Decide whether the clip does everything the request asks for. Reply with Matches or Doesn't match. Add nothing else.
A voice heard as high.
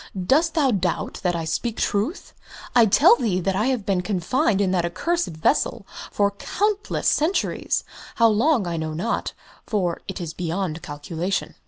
Matches